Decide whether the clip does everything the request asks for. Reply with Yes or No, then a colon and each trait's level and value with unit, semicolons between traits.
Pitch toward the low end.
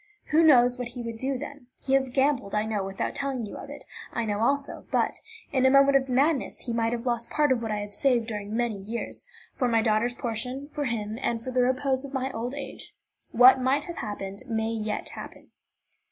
No: high, 245 Hz